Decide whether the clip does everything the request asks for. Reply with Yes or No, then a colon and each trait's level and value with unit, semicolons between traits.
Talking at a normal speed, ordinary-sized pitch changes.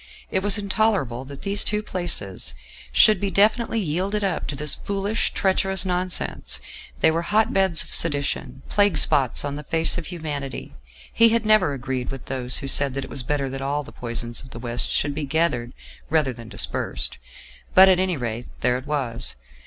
No: average, 190 wpm; wide, 6.4 semitones